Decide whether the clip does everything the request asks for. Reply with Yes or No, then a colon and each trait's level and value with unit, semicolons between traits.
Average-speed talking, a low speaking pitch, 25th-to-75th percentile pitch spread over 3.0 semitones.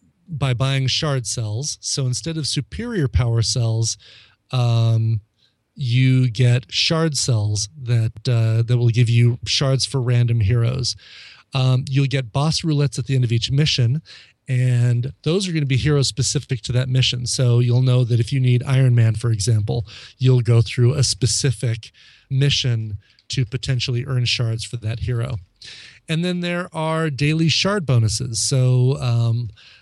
No: average, 160 wpm; low, 125 Hz; average, 2.7 semitones